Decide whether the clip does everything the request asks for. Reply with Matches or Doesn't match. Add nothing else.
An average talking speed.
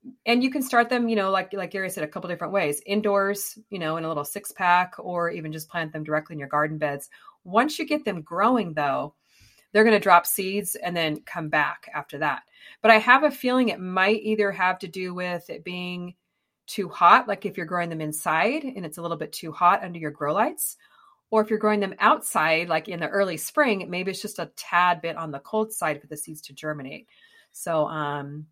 Doesn't match